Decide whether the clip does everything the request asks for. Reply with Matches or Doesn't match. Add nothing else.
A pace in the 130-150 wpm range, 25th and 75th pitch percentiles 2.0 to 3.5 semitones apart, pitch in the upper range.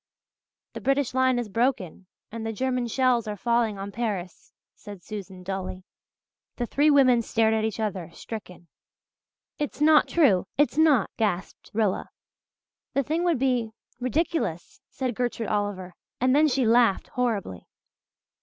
Doesn't match